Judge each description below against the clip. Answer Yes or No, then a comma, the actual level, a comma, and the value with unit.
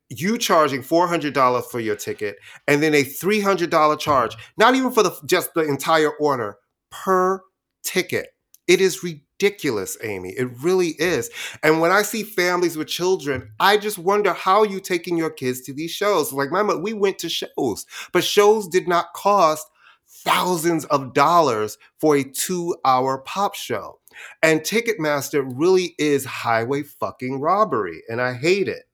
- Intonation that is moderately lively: No, wide, 5.7 semitones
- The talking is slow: No, average, 160 wpm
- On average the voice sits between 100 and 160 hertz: No, medium, 170 Hz